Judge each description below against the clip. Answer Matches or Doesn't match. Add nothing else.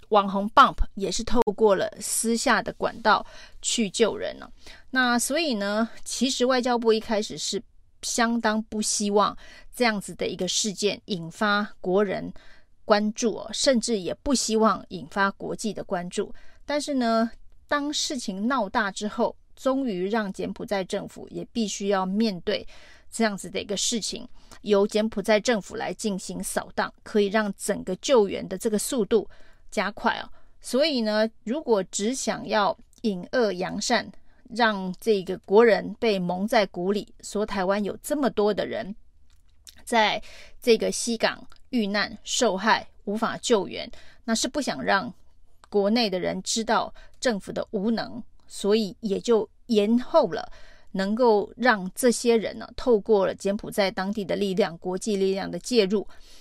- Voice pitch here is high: Matches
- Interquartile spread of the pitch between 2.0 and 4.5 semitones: Matches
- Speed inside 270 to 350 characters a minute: Doesn't match